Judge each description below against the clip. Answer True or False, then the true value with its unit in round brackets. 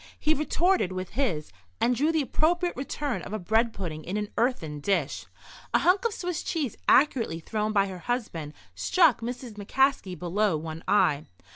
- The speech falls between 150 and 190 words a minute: True (170 wpm)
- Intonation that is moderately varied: False (7.8 semitones)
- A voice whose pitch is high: True (220 Hz)